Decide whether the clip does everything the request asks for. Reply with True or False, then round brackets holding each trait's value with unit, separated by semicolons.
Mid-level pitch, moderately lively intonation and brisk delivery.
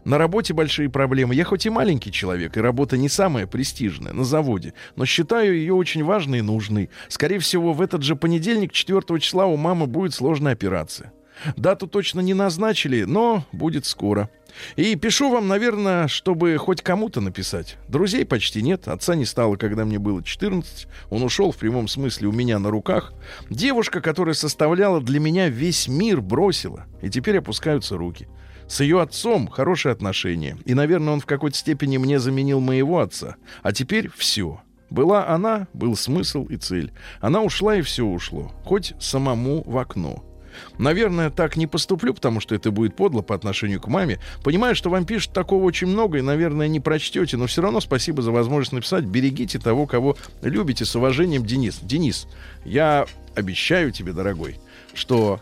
False (145 Hz; 8.1 semitones; 170 wpm)